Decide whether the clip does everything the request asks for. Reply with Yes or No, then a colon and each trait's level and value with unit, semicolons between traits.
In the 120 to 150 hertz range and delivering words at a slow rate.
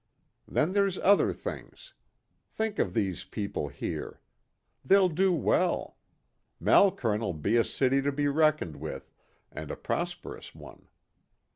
Yes: medium, 140 Hz; slow, 125 wpm